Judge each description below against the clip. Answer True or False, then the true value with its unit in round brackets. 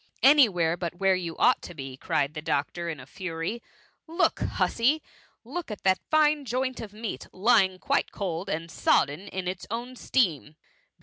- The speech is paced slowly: False (185 wpm)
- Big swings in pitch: True (6.3 semitones)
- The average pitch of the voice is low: False (190 Hz)